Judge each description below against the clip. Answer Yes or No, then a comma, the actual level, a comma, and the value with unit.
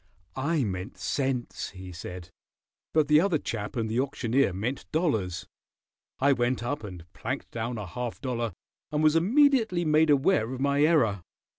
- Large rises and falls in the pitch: Yes, wide, 5.7 semitones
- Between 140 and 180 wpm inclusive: Yes, average, 160 wpm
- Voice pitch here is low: Yes, low, 130 Hz